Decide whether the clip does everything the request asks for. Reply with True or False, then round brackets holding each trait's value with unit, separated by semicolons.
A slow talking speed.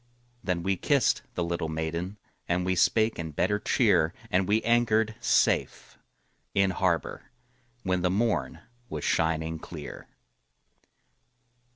True (120 wpm)